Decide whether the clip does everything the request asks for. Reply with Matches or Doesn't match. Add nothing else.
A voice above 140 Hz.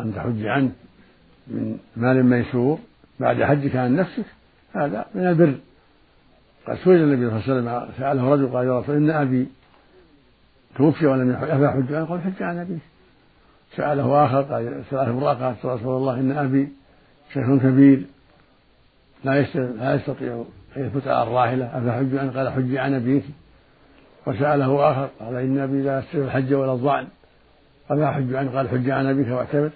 Doesn't match